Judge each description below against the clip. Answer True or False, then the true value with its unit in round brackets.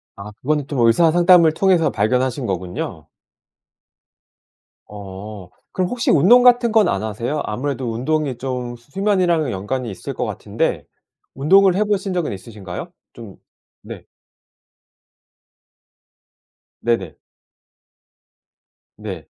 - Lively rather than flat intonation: True (8.2 semitones)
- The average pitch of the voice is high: False (135 Hz)